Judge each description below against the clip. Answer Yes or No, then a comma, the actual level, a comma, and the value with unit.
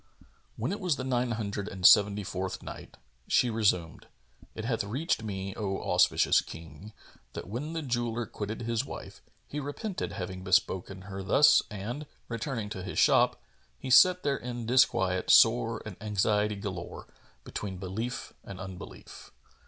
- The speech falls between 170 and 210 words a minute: No, average, 155 wpm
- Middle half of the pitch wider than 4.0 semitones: Yes, average, 4.5 semitones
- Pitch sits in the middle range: No, low, 105 Hz